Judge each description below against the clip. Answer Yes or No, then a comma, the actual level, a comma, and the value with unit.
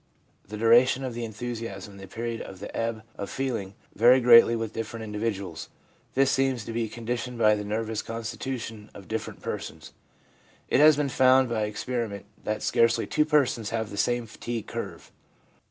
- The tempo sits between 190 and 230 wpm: No, average, 180 wpm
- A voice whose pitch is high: No, low, 115 Hz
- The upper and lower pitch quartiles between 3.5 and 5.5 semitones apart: No, narrow, 2.4 semitones